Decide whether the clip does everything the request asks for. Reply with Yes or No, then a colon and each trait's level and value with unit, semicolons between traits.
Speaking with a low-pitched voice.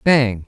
Yes: low, 120 Hz